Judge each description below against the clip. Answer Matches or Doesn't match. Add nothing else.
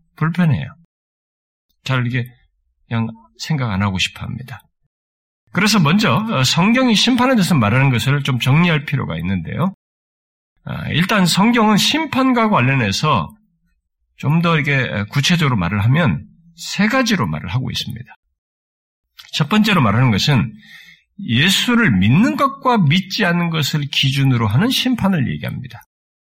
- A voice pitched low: Doesn't match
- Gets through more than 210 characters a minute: Matches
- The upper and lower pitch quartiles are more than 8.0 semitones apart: Matches